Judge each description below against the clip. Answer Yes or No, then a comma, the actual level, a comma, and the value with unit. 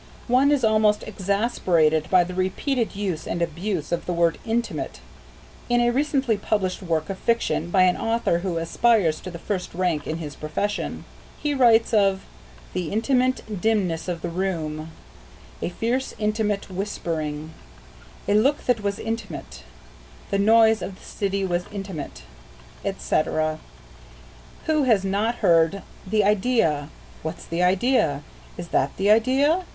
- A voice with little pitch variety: No, average, 4.9 semitones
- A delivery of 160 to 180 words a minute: No, average, 145 wpm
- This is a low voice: No, high, 195 Hz